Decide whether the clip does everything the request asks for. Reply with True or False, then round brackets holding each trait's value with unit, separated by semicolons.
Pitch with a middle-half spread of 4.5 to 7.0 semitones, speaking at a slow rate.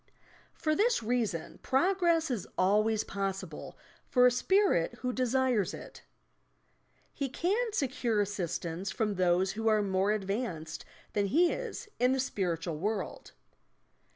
True (5.6 semitones; 125 wpm)